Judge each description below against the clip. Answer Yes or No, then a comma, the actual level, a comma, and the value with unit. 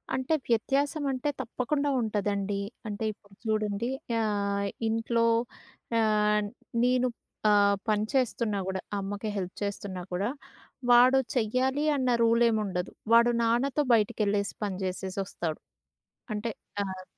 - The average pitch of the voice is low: No, high, 215 Hz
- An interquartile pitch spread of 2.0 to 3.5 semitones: Yes, average, 3.2 semitones